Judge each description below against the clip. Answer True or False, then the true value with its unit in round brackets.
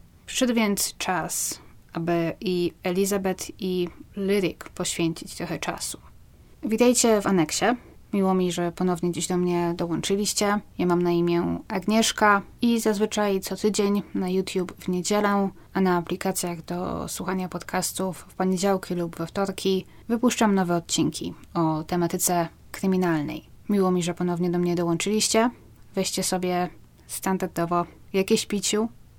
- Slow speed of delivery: False (130 wpm)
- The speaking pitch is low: False (185 Hz)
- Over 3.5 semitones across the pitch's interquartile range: False (2.6 semitones)